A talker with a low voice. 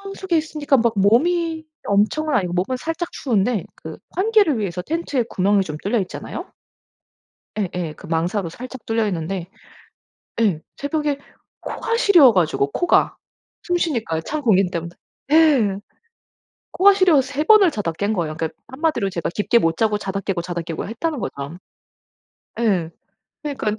No: high, 220 Hz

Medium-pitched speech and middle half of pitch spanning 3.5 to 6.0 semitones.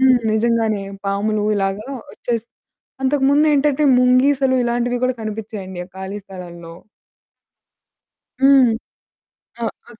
No: high, 235 Hz; average, 4.5 semitones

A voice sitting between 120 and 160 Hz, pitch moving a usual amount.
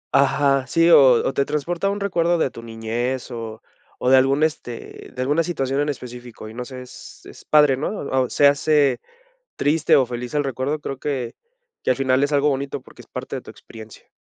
Yes: low, 135 Hz; average, 3.1 semitones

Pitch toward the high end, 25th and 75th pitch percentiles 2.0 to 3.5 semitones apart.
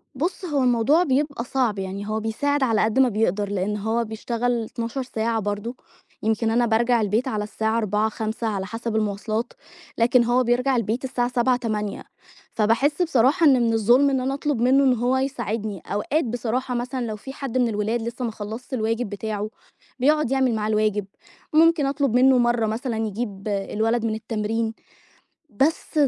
Yes: high, 230 Hz; average, 3.0 semitones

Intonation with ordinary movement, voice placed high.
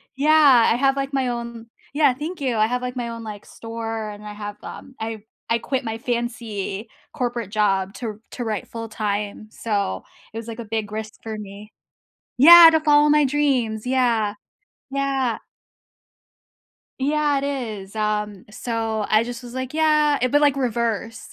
Yes: average, 3.8 semitones; high, 235 Hz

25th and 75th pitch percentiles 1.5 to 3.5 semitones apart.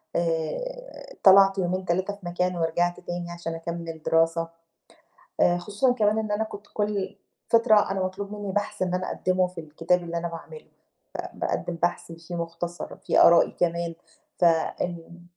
Yes: average, 3.0 semitones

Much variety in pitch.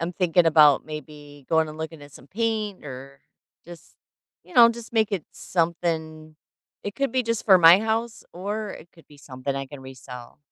Yes: wide, 6.1 semitones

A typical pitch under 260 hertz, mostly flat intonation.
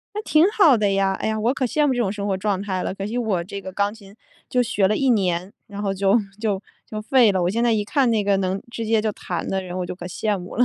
No: high, 205 Hz; average, 3.0 semitones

